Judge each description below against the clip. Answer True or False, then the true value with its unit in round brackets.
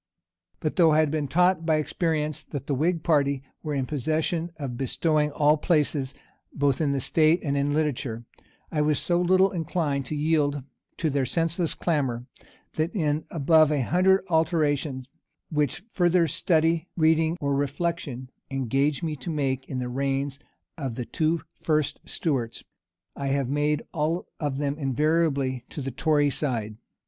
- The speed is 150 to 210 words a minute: True (160 wpm)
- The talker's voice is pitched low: False (150 Hz)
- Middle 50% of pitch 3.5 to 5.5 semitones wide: False (2.8 semitones)